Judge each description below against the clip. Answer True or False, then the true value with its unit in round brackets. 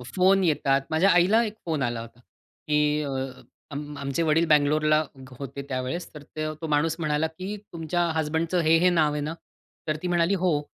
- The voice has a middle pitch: True (155 Hz)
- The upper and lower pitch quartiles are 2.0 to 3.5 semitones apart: True (2.5 semitones)